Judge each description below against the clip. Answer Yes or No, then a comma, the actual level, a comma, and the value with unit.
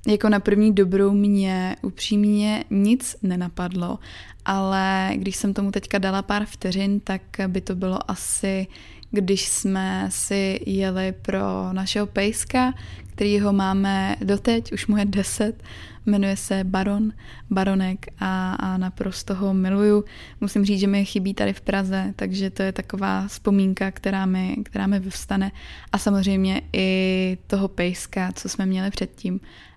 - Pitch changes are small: Yes, narrow, 1.2 semitones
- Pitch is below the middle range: No, high, 195 Hz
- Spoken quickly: No, average, 145 wpm